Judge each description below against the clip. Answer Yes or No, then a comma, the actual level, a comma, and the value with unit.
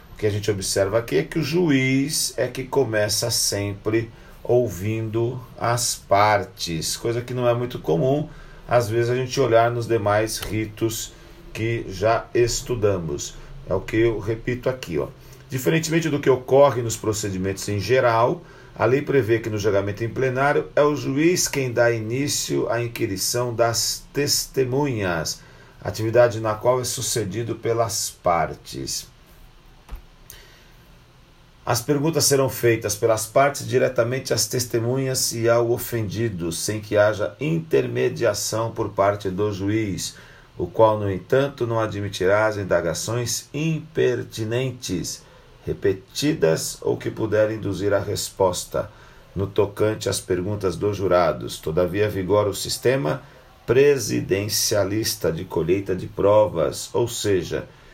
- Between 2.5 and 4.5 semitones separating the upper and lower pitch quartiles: Yes, average, 3.6 semitones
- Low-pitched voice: Yes, low, 115 Hz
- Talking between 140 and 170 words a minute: No, average, 130 wpm